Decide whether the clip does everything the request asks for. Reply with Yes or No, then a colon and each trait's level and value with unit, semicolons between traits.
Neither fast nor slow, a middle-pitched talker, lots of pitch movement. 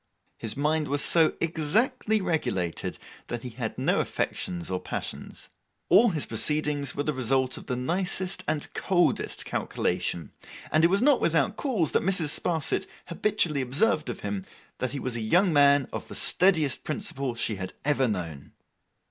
Yes: average, 165 wpm; medium, 150 Hz; wide, 5.8 semitones